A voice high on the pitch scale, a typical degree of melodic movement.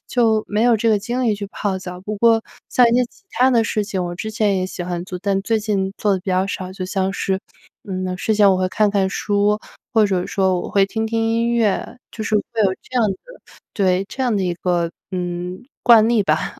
Yes: high, 205 Hz; average, 3.0 semitones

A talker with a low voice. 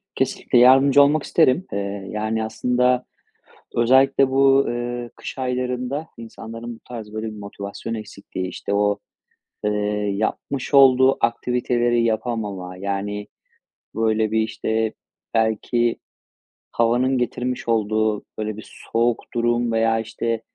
Yes: low, 115 Hz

